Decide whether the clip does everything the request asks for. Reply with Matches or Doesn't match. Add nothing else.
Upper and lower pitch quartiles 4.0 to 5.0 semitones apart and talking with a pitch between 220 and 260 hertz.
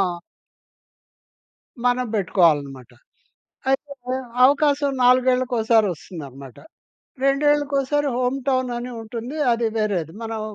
Matches